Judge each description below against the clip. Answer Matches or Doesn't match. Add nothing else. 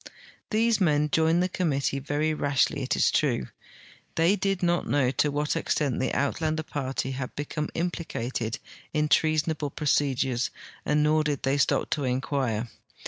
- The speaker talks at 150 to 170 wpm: Matches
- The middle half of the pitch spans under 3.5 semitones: Matches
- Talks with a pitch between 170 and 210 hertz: Doesn't match